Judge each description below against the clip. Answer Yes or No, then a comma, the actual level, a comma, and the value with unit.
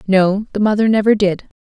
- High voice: Yes, high, 205 Hz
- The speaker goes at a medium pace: Yes, average, 185 wpm